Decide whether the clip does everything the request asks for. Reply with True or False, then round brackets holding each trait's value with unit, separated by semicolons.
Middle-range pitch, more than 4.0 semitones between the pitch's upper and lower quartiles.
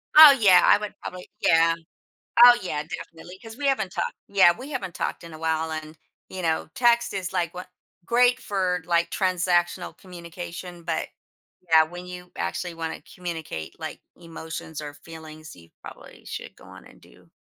False (175 Hz; 2.6 semitones)